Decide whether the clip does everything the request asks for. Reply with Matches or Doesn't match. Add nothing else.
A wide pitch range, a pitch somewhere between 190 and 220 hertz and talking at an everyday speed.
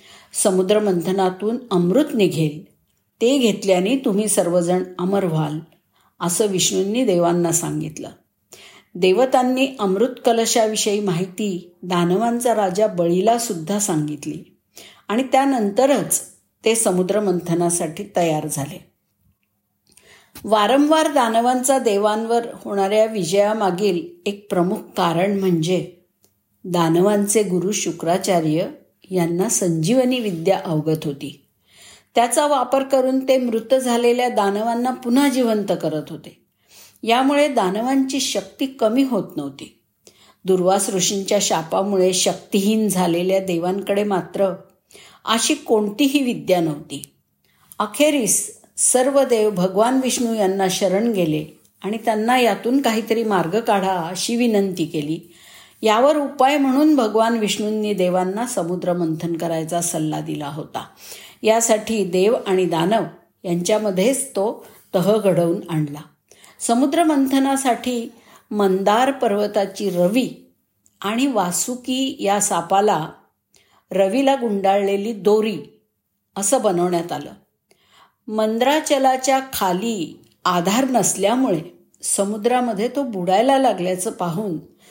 Doesn't match